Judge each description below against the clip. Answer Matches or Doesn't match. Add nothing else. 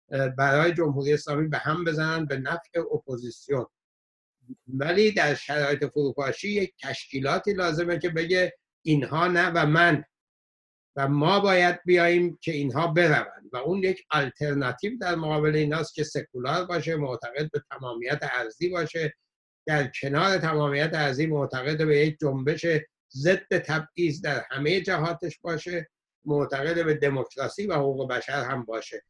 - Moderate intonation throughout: Matches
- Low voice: Doesn't match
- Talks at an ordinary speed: Matches